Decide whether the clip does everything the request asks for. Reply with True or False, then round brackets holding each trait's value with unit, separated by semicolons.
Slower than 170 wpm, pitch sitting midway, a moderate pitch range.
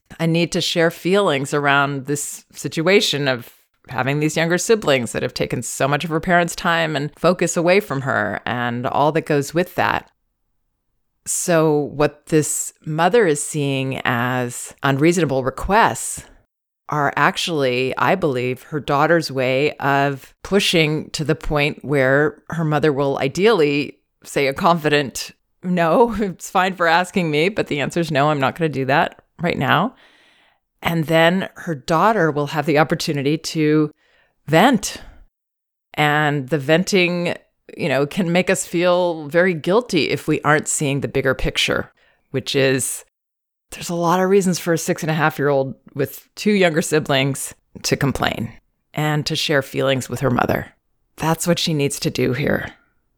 True (160 wpm; 155 Hz; 3.6 semitones)